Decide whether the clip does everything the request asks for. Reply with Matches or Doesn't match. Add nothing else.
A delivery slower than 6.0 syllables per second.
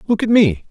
Matches